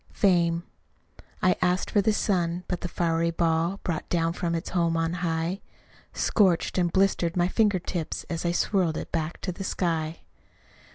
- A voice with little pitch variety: Yes, narrow, 1.7 semitones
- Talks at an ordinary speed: Yes, average, 170 wpm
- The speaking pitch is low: No, medium, 175 Hz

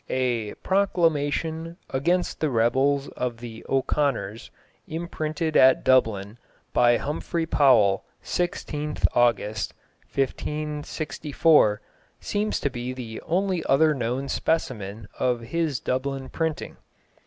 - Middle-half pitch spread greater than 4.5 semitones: Yes, average, 4.9 semitones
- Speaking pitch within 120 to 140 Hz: Yes, low, 135 Hz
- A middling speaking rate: No, slow, 100 wpm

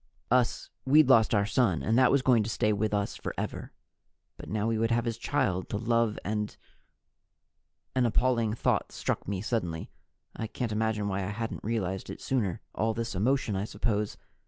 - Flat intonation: Yes, narrow, 2.3 semitones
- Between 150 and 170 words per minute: No, average, 180 wpm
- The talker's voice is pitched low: Yes, low, 110 Hz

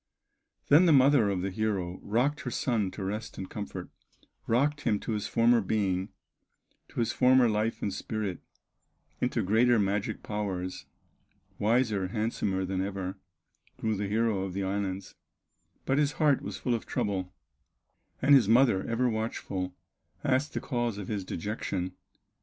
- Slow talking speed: No, average, 150 wpm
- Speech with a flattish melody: No, average, 3.8 semitones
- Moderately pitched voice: No, low, 105 Hz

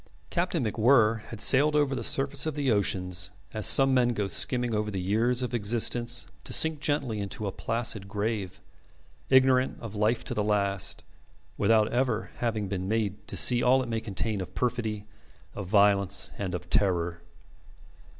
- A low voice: Yes, low, 110 Hz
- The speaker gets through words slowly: No, average, 170 wpm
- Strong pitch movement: No, average, 3.7 semitones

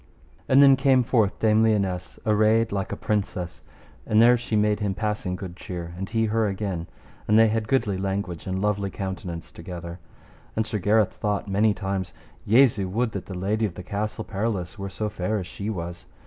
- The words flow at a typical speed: Yes, average, 190 wpm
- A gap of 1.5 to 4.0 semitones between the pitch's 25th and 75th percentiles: Yes, average, 2.8 semitones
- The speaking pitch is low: Yes, low, 105 Hz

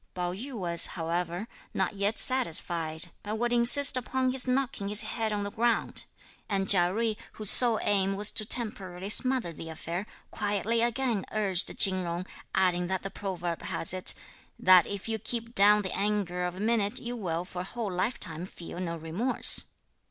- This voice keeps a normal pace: Yes, average, 180 wpm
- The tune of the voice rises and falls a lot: No, average, 4.2 semitones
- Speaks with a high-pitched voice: Yes, high, 200 Hz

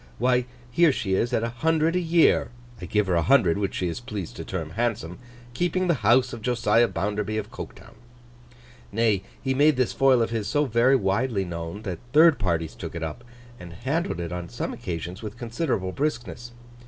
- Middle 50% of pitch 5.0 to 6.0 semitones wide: Yes, wide, 5.5 semitones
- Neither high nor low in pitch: No, low, 115 Hz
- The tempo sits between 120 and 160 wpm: No, average, 195 wpm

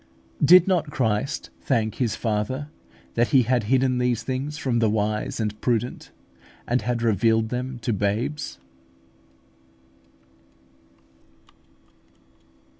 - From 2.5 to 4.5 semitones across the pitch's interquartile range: Yes, average, 3.1 semitones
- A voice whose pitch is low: Yes, low, 120 Hz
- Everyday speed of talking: No, slow, 110 wpm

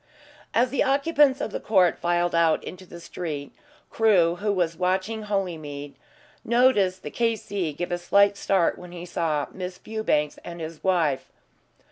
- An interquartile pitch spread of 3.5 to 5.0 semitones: Yes, average, 3.8 semitones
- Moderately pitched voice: Yes, medium, 180 Hz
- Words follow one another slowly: No, average, 155 wpm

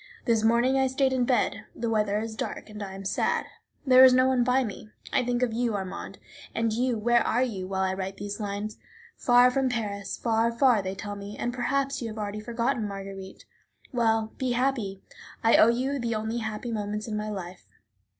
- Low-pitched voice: No, high, 225 Hz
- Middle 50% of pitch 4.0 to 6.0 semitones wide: No, average, 3.2 semitones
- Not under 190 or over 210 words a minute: Yes, fast, 205 wpm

